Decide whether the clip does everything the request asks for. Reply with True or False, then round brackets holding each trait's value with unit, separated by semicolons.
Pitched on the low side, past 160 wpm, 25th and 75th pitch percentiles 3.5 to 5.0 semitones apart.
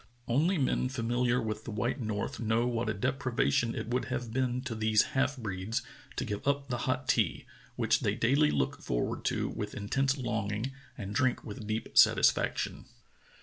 False (120 Hz; 175 wpm; 3.1 semitones)